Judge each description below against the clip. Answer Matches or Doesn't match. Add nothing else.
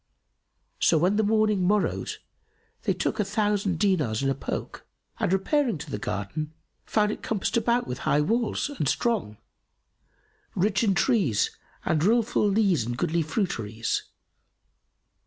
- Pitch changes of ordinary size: Doesn't match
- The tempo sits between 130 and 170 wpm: Matches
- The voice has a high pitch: Matches